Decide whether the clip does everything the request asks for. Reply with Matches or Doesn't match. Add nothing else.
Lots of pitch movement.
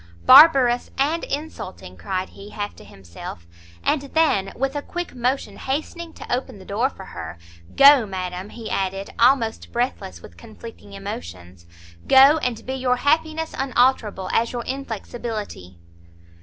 Matches